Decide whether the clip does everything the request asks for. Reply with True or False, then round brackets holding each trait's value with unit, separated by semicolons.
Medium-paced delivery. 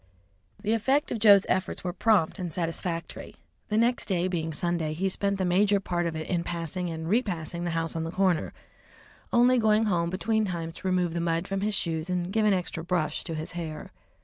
False (210 wpm)